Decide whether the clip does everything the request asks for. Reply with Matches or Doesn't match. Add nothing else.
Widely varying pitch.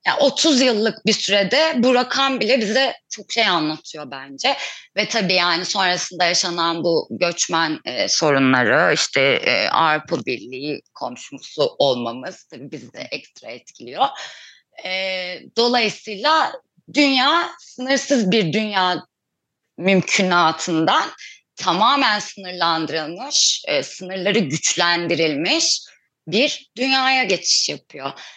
Matches